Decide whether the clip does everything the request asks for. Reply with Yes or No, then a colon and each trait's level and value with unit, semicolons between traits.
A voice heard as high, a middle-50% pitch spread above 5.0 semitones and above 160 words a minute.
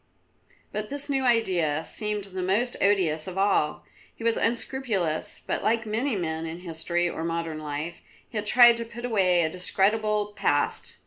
Yes: high, 195 Hz; wide, 5.4 semitones; average, 170 wpm